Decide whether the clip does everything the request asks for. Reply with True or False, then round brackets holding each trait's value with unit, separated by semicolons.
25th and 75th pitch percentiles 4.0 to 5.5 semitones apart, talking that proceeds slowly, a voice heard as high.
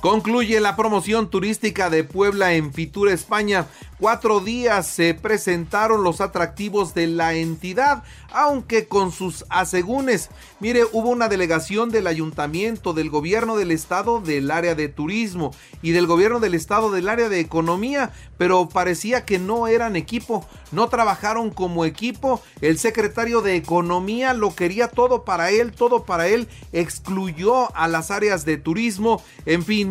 False (5.0 semitones; 150 wpm; 200 Hz)